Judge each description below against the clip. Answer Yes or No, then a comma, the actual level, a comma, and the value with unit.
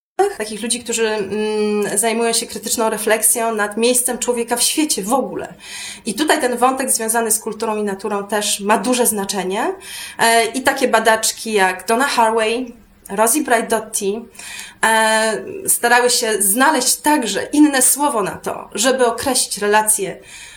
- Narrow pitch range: Yes, narrow, 2.3 semitones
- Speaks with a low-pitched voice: No, high, 230 Hz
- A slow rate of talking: No, average, 135 wpm